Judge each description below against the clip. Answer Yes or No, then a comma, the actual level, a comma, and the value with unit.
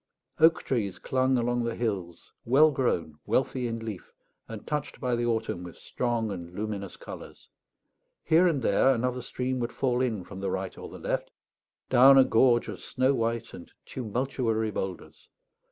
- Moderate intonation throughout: Yes, average, 3.3 semitones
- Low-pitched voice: Yes, low, 120 Hz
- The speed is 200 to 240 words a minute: No, average, 170 wpm